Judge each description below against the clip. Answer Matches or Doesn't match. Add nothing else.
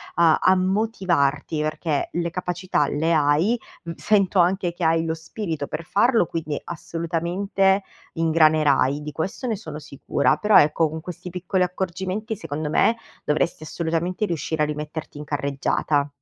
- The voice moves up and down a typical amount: Matches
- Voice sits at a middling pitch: Matches